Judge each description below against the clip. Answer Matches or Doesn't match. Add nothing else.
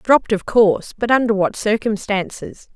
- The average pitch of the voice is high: Matches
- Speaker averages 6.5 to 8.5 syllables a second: Doesn't match